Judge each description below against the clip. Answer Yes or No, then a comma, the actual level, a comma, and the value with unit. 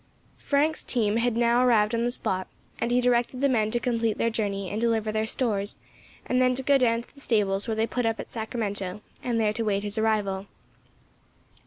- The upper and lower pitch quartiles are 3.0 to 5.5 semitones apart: No, narrow, 2.5 semitones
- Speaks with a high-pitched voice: Yes, high, 225 Hz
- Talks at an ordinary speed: No, fast, 210 wpm